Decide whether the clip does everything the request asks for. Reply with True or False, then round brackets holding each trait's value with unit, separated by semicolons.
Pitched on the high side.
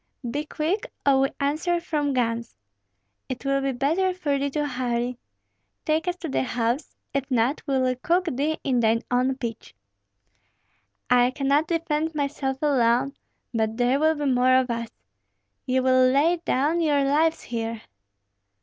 True (275 Hz)